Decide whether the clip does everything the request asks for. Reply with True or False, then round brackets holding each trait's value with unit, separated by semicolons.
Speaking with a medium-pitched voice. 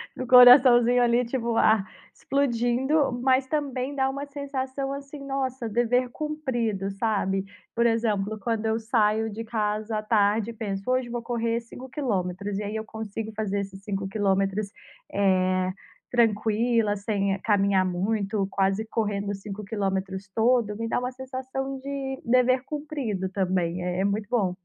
False (225 Hz)